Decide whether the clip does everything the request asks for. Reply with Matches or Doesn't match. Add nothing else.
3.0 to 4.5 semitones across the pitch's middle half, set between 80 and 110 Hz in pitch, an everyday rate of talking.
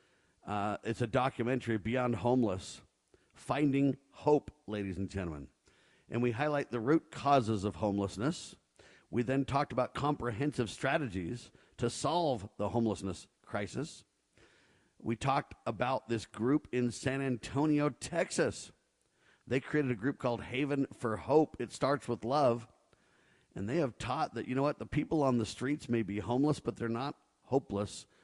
Doesn't match